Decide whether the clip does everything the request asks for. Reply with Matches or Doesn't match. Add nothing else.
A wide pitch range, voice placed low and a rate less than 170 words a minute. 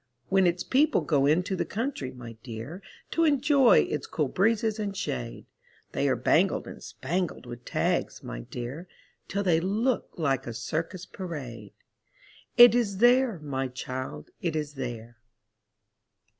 Doesn't match